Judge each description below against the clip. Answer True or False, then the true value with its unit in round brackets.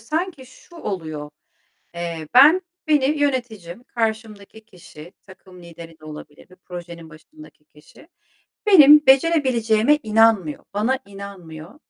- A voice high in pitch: True (215 Hz)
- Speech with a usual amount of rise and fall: False (7.7 semitones)